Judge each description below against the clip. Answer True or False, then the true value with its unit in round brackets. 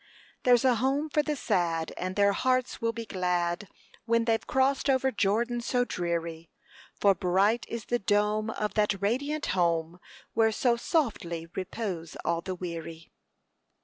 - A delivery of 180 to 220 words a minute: False (150 wpm)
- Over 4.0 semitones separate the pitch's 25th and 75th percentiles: True (5.4 semitones)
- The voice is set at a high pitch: True (210 Hz)